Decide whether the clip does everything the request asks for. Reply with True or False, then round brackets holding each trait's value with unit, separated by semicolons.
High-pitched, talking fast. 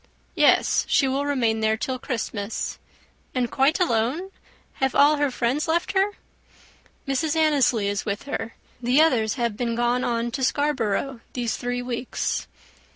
False (250 Hz; 150 wpm)